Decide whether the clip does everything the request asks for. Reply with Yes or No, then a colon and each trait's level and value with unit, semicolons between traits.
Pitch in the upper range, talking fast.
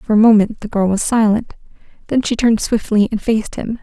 Yes: high, 215 Hz; fast, 220 wpm